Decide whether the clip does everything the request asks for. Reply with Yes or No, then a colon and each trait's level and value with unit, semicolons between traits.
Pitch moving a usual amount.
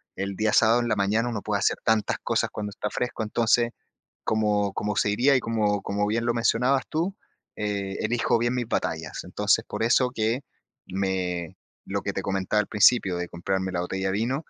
Yes: average, 3.2 semitones